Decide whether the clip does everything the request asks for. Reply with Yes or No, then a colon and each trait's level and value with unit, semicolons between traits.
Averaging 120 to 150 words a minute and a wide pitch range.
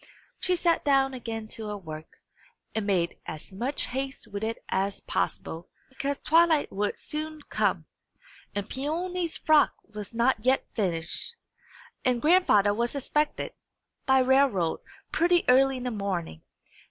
Yes: average, 140 wpm; wide, 6.3 semitones